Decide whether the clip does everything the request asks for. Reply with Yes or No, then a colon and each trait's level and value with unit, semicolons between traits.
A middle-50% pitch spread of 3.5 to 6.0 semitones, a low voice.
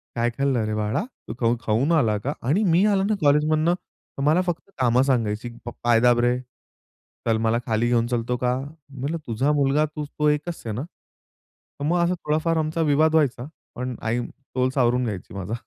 Yes: average, 4.6 semitones; low, 130 Hz